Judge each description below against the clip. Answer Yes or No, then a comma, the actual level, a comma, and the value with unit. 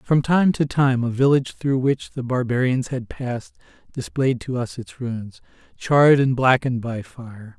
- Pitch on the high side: No, low, 125 Hz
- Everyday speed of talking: Yes, average, 175 wpm